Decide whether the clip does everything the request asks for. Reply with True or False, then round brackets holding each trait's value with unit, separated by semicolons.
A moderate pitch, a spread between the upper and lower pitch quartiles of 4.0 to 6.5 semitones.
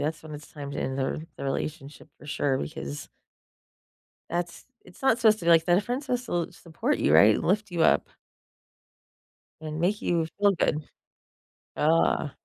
True (160 Hz; 4.3 semitones)